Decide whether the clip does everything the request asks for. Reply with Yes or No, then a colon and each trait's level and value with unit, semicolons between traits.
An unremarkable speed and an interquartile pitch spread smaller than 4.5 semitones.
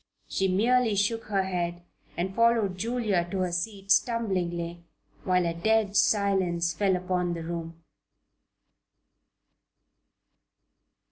No: slow, 110 wpm; average, 3.4 semitones